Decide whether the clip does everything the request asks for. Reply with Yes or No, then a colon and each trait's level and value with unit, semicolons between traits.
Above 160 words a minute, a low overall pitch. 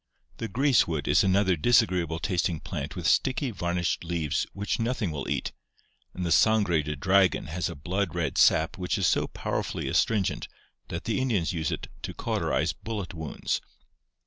Yes: average, 170 wpm; very low, 90 Hz